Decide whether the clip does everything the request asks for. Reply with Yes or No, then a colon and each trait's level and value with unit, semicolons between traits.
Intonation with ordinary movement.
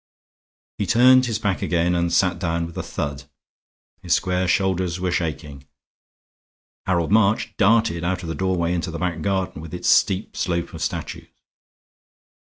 No: narrow, 2.3 semitones